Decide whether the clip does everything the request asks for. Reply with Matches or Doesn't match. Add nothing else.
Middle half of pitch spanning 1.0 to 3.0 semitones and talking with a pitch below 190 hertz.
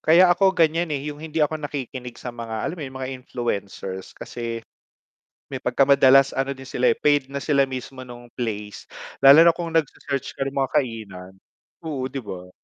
Doesn't match